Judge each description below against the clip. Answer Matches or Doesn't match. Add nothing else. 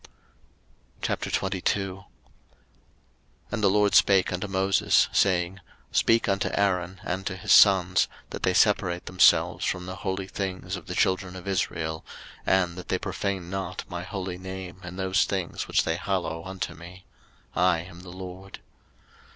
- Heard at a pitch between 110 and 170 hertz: Doesn't match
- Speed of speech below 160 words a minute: Matches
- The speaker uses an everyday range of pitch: Doesn't match